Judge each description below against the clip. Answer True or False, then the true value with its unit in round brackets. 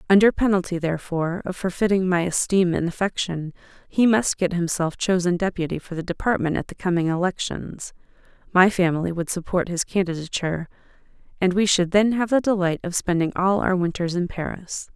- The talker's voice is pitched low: False (180 Hz)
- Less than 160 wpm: False (170 wpm)